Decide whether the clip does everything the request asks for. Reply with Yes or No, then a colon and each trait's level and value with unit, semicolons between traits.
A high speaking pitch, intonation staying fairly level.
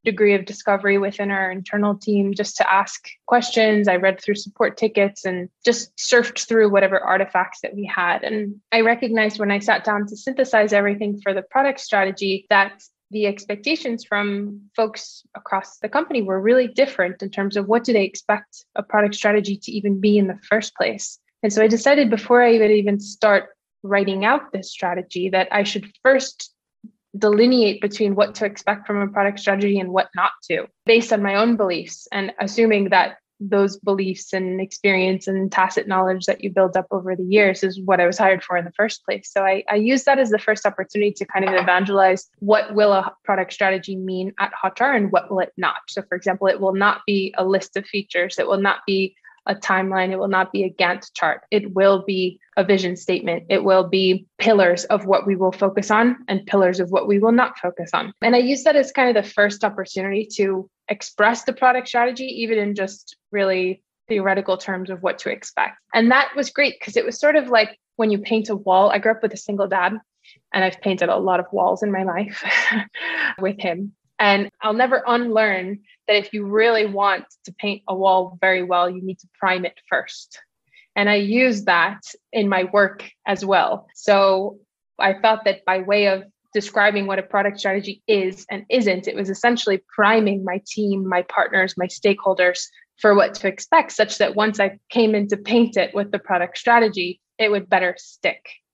Yes: high, 200 Hz; narrow, 2.1 semitones